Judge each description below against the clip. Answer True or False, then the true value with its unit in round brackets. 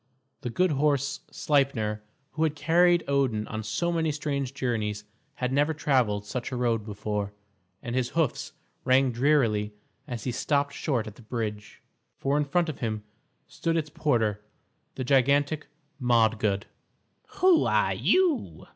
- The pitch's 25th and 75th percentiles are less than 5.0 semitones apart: False (5.3 semitones)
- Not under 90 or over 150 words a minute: True (145 wpm)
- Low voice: True (130 Hz)